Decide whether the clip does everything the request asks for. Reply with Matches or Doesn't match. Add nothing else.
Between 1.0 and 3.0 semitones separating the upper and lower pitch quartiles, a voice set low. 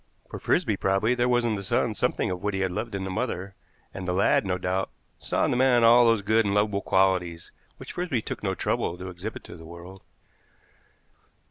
Doesn't match